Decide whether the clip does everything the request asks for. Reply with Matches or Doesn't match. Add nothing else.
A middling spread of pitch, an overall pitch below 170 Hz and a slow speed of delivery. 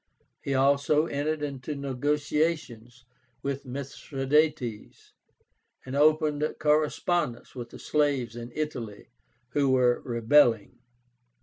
Matches